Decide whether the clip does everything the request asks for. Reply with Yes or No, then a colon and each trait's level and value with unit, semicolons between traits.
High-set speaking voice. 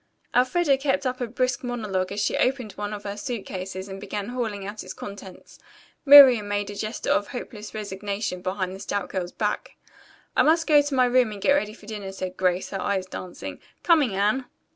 Yes: high, 210 Hz